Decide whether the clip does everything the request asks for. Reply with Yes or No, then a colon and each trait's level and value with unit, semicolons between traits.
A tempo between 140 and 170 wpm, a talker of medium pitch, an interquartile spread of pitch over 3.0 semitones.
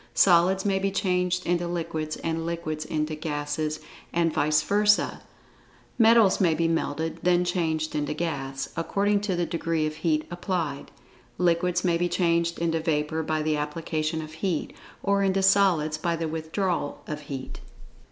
No: average, 155 wpm; medium, 165 Hz; narrow, 2.6 semitones